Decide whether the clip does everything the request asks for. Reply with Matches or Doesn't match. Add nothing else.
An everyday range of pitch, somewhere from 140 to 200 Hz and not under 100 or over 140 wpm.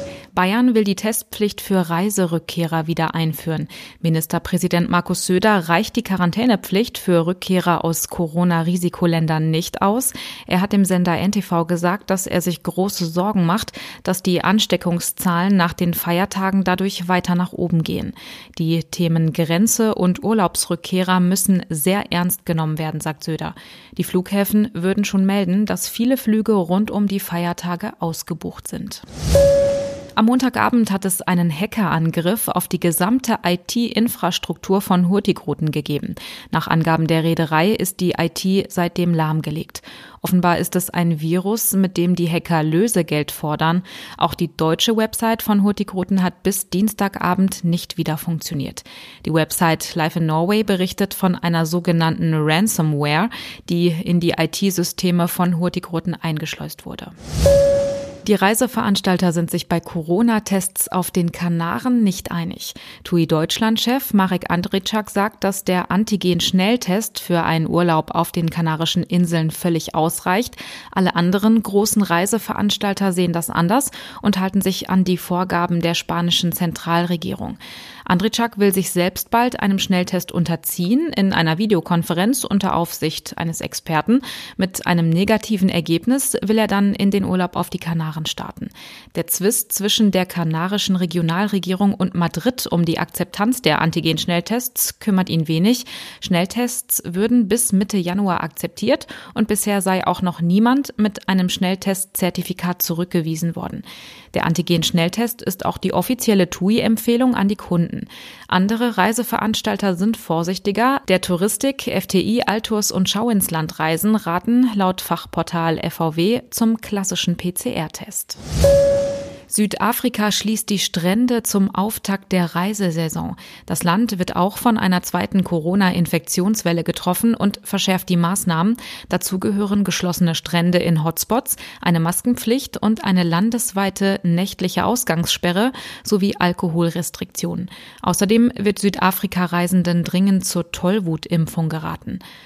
Matches